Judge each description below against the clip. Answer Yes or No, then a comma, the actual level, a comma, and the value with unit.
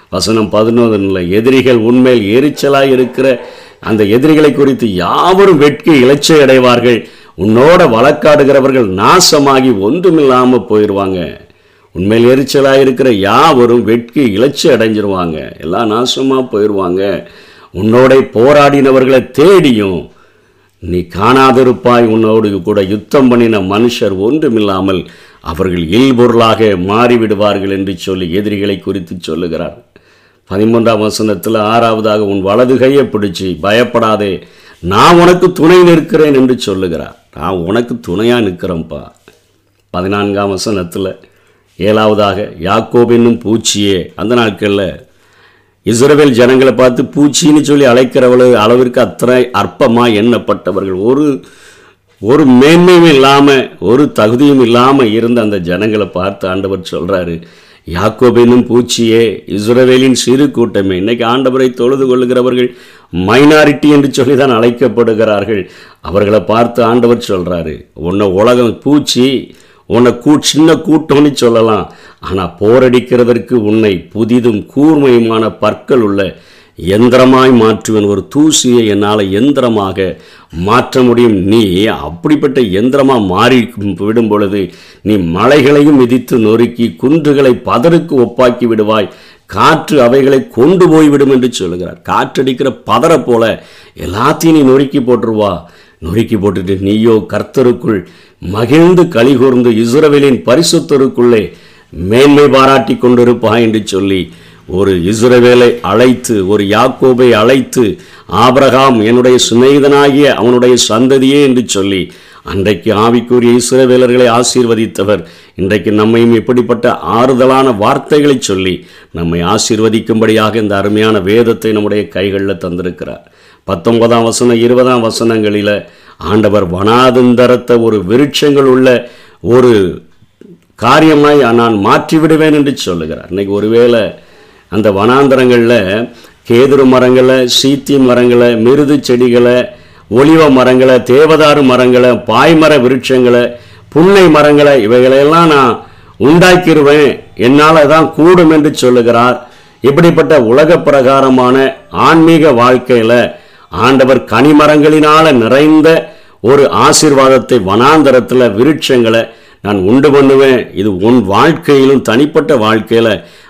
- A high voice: No, low, 120 Hz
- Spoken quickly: No, average, 95 wpm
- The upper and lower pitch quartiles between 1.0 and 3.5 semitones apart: No, average, 4.0 semitones